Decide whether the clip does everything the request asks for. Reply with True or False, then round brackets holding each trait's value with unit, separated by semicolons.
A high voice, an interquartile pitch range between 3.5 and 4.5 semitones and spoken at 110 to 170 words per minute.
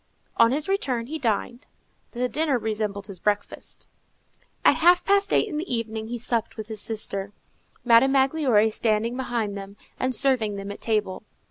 True (230 Hz; 3.9 semitones; 165 wpm)